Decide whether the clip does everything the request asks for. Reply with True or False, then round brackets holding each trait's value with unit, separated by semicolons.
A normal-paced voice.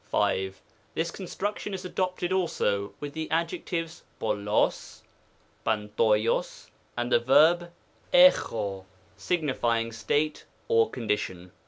False (105 wpm)